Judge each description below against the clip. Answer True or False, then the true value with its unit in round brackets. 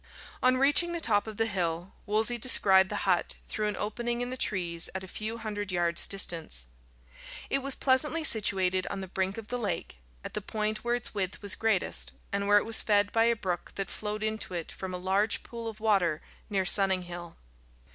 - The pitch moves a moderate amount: True (3.2 semitones)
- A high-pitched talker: True (205 Hz)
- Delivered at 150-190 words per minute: False (205 wpm)